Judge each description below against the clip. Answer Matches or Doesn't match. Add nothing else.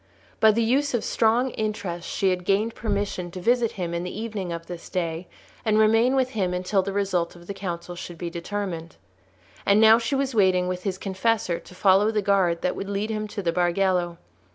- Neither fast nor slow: Doesn't match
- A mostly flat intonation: Doesn't match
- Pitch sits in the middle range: Doesn't match